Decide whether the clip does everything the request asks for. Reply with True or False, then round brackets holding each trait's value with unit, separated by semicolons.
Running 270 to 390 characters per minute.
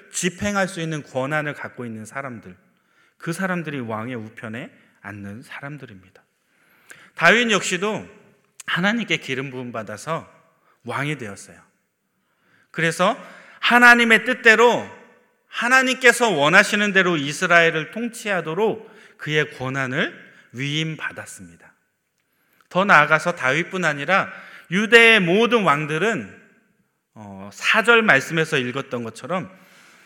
False (260 characters per minute)